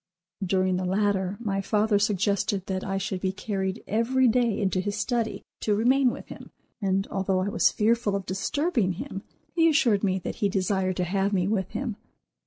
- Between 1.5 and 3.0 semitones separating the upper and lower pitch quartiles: Yes, narrow, 2.6 semitones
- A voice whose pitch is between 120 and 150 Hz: No, high, 200 Hz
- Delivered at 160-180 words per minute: No, average, 190 wpm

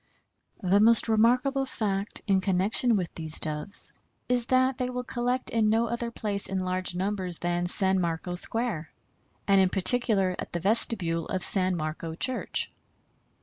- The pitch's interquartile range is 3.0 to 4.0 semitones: No, average, 4.6 semitones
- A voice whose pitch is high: Yes, high, 195 Hz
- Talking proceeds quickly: No, average, 155 wpm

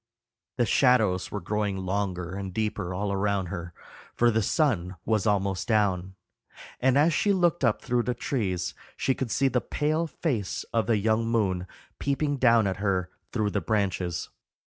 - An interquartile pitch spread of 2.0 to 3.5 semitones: No, average, 4.5 semitones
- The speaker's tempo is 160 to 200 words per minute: Yes, average, 170 wpm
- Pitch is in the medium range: No, low, 105 Hz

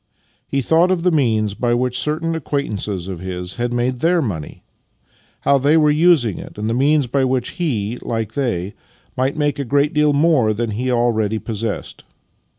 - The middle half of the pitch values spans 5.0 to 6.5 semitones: Yes, average, 5.3 semitones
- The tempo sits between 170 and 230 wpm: Yes, average, 185 wpm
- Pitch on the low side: Yes, low, 125 Hz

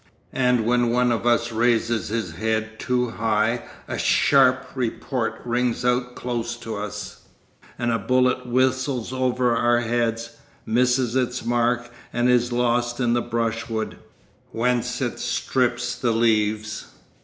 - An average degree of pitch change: No, narrow, 1.4 semitones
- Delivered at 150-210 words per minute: No, slow, 135 wpm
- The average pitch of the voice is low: Yes, low, 120 Hz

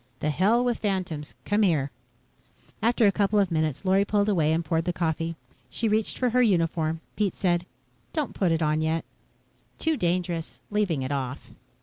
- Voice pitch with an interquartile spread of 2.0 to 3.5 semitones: No, average, 4.5 semitones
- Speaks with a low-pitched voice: No, medium, 175 Hz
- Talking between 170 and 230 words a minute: Yes, average, 180 wpm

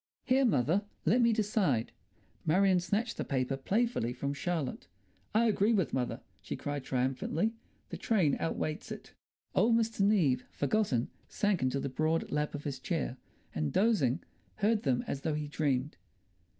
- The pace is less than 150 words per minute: No, average, 155 wpm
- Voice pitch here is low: No, medium, 155 Hz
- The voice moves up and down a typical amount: No, wide, 7.8 semitones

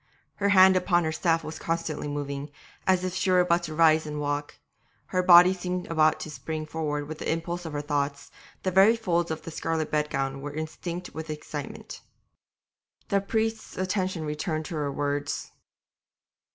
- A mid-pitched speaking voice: Yes, medium, 160 Hz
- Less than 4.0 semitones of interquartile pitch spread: Yes, average, 3.3 semitones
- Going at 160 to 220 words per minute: Yes, average, 175 wpm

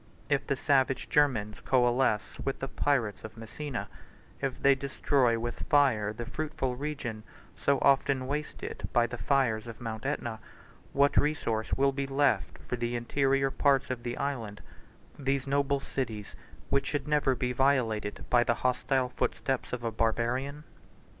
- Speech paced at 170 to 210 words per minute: No, average, 155 wpm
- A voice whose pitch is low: Yes, low, 130 Hz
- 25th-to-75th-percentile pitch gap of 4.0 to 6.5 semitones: No, average, 2.9 semitones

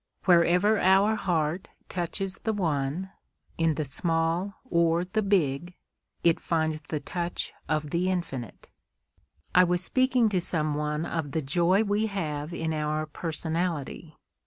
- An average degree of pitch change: Yes, average, 3.4 semitones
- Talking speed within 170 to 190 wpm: No, slow, 135 wpm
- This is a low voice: No, medium, 170 Hz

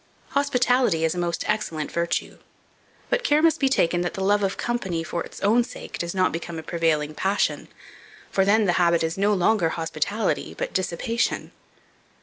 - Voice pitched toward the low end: No, medium, 185 Hz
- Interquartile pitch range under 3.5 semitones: No, average, 4.7 semitones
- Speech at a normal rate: Yes, average, 175 wpm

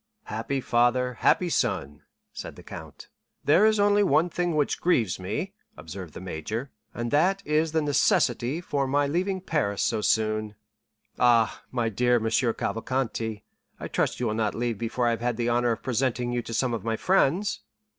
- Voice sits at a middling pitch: No, low, 120 Hz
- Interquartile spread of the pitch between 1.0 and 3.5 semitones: No, average, 5.1 semitones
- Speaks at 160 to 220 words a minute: Yes, average, 180 wpm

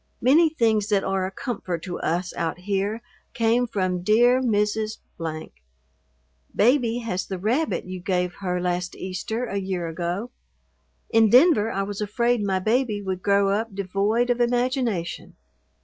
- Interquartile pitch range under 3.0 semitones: No, average, 4.1 semitones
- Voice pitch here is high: Yes, high, 205 Hz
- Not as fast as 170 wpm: Yes, average, 150 wpm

